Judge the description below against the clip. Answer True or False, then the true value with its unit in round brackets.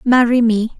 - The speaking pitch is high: True (235 Hz)